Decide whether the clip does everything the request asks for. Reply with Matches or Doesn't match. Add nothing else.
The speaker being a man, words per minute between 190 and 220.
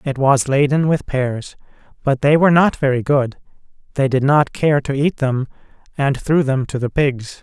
Matches